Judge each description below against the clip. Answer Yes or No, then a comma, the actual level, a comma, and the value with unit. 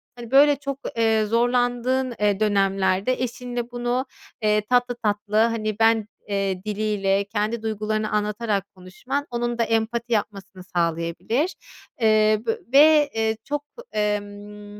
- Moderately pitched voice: No, high, 220 Hz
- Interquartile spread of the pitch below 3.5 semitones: Yes, average, 2.8 semitones